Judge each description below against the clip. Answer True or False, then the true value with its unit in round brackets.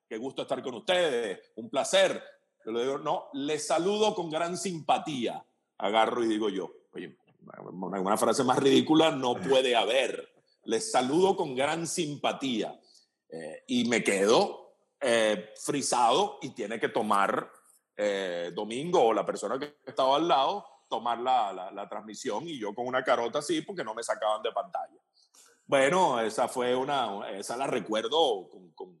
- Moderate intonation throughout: False (8.0 semitones)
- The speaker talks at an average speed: True (160 wpm)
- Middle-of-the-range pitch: False (130 Hz)